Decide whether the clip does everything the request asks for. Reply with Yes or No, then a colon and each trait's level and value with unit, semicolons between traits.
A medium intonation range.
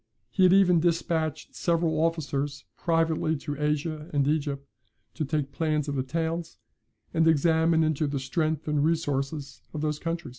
No: narrow, 2.2 semitones